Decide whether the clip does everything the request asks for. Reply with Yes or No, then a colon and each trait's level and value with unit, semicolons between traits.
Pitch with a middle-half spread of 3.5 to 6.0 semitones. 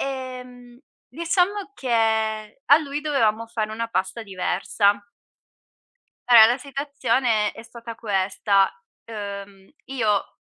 Yes: average, 3.9 semitones